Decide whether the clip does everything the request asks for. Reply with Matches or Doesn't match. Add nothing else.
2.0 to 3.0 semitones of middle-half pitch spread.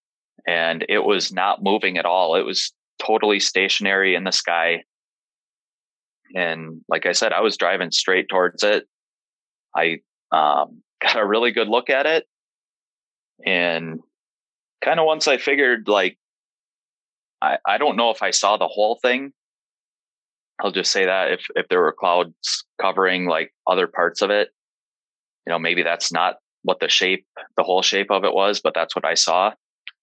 Doesn't match